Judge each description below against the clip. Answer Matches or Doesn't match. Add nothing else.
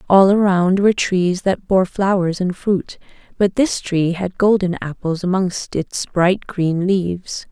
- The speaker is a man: Doesn't match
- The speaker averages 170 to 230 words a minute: Doesn't match